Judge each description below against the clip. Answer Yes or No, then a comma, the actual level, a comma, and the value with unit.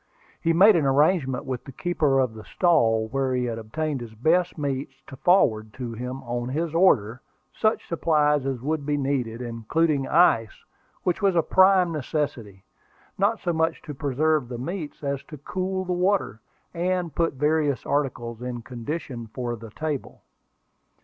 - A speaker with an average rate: Yes, average, 165 wpm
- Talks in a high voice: No, medium, 140 Hz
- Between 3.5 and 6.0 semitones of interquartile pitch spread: Yes, average, 5.2 semitones